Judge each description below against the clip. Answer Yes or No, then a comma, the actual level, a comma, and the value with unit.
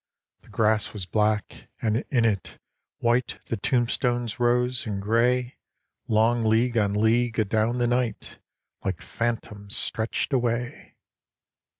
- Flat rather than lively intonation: Yes, narrow, 2.1 semitones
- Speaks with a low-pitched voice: Yes, low, 115 Hz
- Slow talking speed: Yes, slow, 120 wpm